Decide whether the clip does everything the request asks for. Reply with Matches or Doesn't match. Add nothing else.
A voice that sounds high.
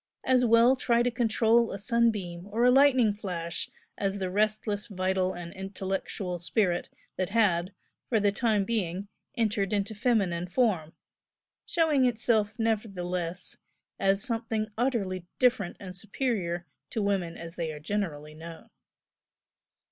Matches